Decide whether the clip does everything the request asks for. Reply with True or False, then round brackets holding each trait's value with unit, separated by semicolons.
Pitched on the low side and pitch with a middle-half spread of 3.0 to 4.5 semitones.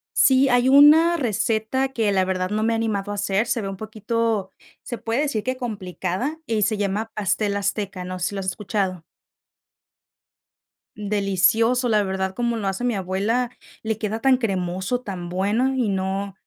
False (210 Hz; 3.6 semitones)